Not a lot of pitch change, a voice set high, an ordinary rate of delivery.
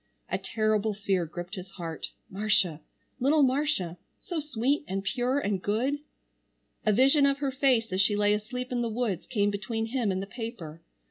No: average, 4.8 semitones; high, 215 Hz; average, 180 wpm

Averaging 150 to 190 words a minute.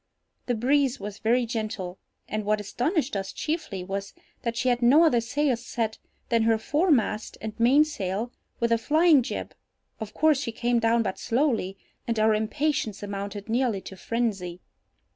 Yes: average, 160 wpm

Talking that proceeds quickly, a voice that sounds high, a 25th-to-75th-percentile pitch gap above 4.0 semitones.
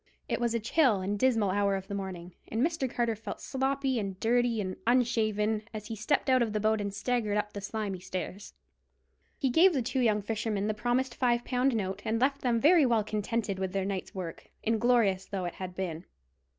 No: fast, 210 wpm; high, 220 Hz; average, 3.6 semitones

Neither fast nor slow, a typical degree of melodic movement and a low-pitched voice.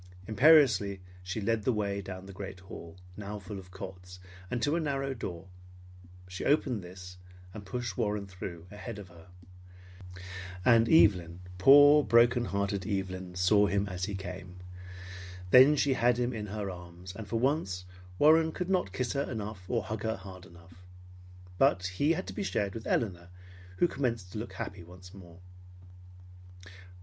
Yes: average, 165 wpm; average, 4.7 semitones; low, 100 Hz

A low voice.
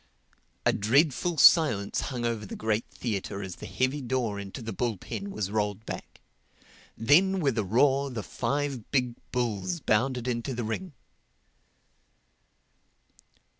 Yes: low, 120 Hz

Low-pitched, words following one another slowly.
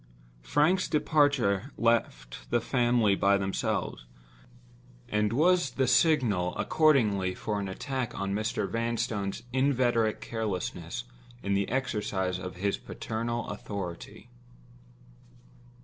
Yes: low, 110 Hz; slow, 100 wpm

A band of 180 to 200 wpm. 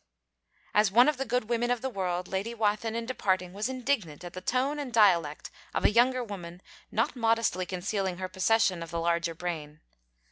Yes: average, 190 wpm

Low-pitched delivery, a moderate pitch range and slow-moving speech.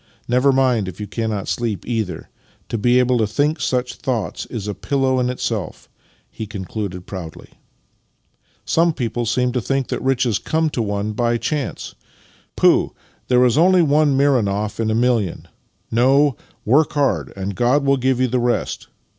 No: low, 125 Hz; average, 3.8 semitones; average, 170 wpm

